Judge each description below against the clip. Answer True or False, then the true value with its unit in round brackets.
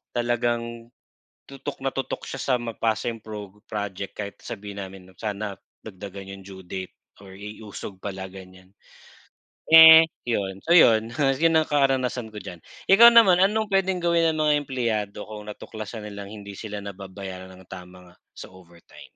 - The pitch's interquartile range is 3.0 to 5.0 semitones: False (5.4 semitones)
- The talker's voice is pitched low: True (105 Hz)